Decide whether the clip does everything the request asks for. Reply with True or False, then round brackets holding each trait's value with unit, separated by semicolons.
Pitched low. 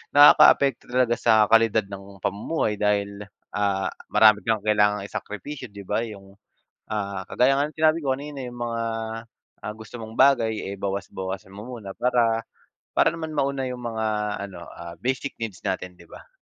True (110 Hz)